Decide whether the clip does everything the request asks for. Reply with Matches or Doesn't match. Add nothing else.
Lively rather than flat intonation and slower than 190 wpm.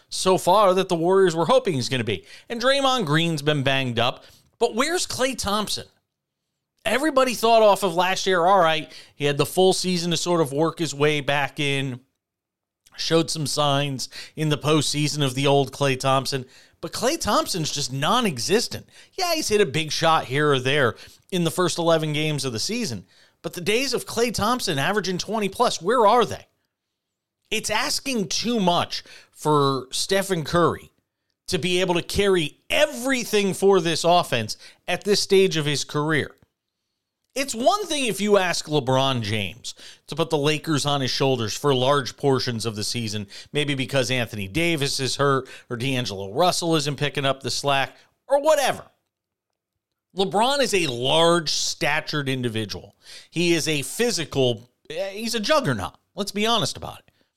Matches